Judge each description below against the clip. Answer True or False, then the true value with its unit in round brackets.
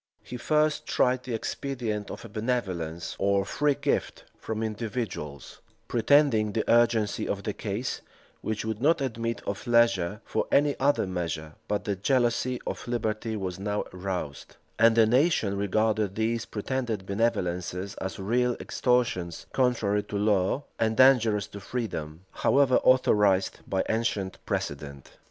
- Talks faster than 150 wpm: False (140 wpm)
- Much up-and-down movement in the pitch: False (3.8 semitones)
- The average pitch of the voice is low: True (110 Hz)